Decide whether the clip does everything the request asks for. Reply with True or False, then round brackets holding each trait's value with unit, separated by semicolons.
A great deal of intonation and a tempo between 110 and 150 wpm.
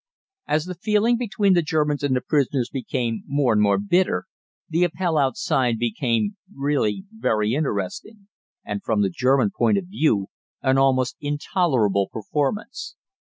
True (7.2 semitones; 145 wpm)